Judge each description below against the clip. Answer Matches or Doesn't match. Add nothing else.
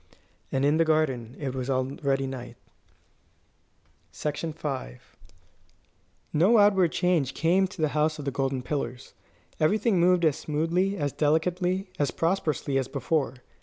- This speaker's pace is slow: Matches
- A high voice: Doesn't match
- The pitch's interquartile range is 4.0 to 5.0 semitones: Matches